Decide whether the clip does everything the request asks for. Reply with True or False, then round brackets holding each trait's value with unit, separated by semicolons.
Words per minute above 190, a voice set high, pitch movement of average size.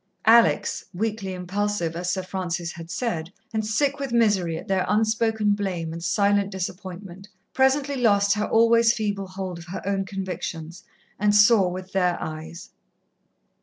False (150 wpm; 195 Hz; 3.3 semitones)